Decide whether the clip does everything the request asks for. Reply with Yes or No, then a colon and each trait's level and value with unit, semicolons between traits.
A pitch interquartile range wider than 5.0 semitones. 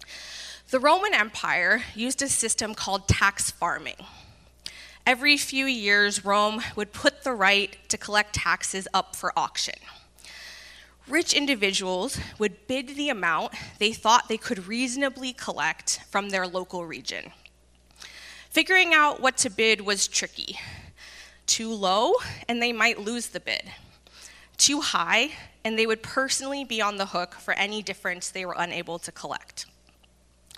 Yes: wide, 5.6 semitones